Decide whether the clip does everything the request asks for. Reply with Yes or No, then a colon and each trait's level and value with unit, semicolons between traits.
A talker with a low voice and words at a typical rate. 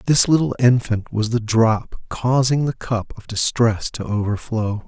Yes: low, 115 Hz; average, 160 wpm